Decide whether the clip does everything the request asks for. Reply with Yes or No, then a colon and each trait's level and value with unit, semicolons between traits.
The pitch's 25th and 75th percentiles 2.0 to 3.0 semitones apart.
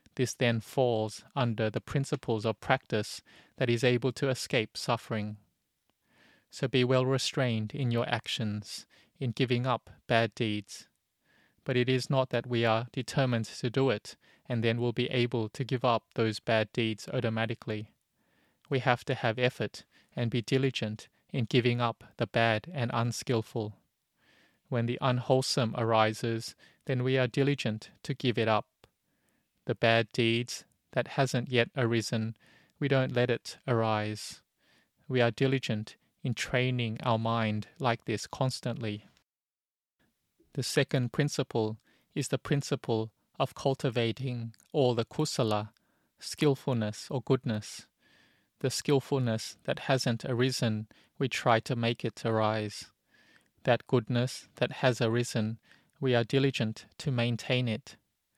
Yes: average, 2.7 semitones